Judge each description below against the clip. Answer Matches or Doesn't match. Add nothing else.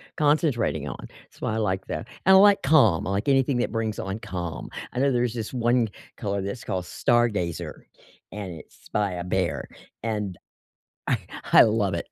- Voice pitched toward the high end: Doesn't match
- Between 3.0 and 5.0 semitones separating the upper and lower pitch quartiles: Matches